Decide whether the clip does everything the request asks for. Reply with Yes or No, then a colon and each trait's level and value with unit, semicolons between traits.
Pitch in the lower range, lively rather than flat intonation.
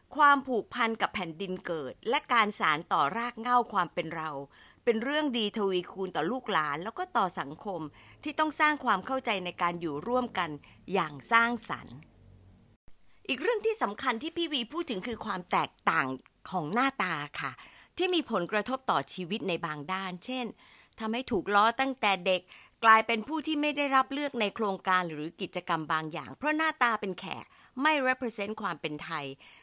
No: high, 210 Hz; wide, 6.8 semitones